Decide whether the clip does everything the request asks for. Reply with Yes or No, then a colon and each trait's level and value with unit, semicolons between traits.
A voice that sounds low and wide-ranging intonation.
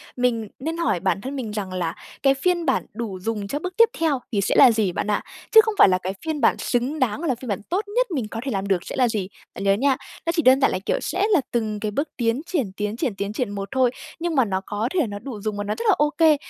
No: high, 235 Hz; wide, 6.1 semitones